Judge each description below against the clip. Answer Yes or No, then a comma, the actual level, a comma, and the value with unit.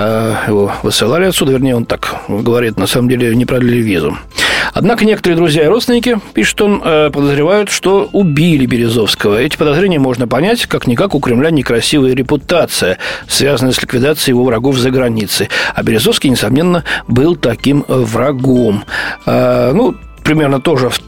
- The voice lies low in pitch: Yes, low, 130 Hz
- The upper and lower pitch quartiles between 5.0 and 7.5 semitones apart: Yes, average, 5.3 semitones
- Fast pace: No, average, 140 wpm